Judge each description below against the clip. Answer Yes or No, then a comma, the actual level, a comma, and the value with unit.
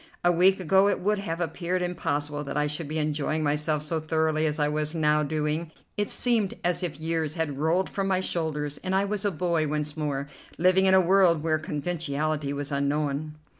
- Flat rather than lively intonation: No, average, 3.1 semitones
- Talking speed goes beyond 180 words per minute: Yes, fast, 205 wpm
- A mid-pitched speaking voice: Yes, medium, 155 Hz